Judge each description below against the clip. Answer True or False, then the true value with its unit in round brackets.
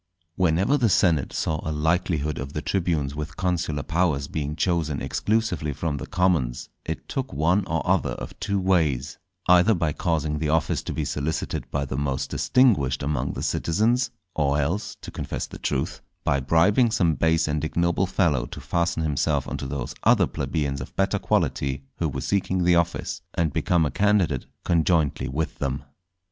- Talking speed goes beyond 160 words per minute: True (175 wpm)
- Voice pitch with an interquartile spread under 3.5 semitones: False (3.8 semitones)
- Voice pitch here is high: False (80 Hz)